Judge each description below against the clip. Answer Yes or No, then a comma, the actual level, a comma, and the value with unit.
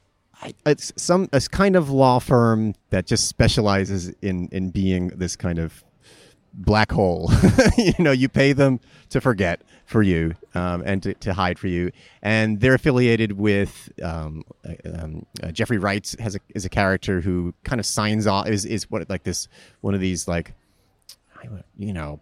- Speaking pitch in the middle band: No, low, 100 Hz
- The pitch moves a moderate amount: Yes, average, 4.3 semitones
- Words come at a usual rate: Yes, average, 175 wpm